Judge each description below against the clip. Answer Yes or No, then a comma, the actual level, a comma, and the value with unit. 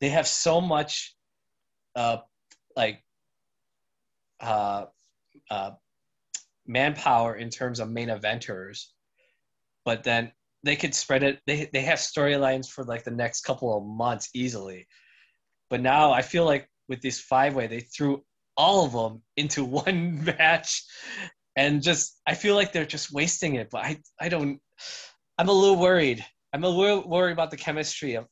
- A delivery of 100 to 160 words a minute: Yes, average, 155 wpm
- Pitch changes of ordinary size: Yes, average, 5.0 semitones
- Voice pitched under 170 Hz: Yes, low, 135 Hz